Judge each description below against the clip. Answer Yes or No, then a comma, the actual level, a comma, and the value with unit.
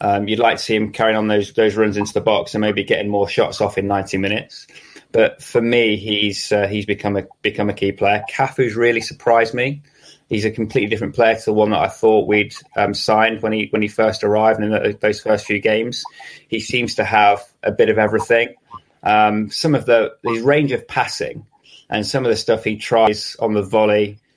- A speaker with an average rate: No, fast, 225 wpm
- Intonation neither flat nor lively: No, narrow, 1.5 semitones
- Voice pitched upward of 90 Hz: Yes, low, 110 Hz